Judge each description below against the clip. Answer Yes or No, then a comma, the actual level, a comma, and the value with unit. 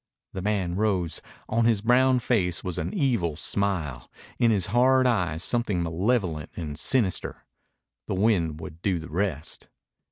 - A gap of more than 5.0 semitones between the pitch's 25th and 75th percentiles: Yes, wide, 5.6 semitones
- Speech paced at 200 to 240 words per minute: No, average, 150 wpm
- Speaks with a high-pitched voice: No, very low, 95 Hz